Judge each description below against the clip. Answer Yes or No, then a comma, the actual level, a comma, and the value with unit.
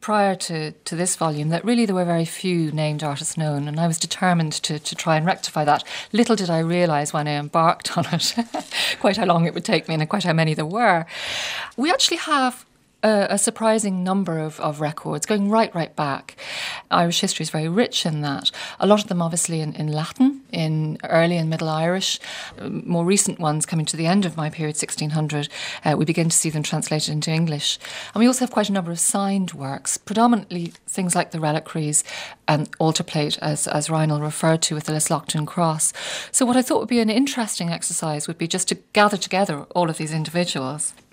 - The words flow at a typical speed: No, fast, 215 wpm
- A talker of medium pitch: Yes, medium, 170 Hz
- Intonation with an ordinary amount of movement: Yes, average, 4.0 semitones